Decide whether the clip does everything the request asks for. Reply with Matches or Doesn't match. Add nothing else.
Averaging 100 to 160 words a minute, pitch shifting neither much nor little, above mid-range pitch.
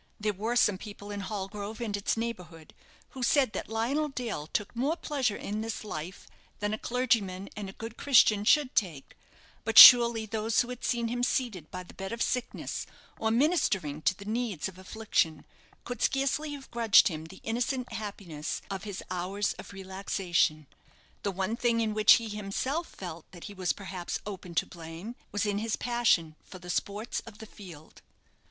Doesn't match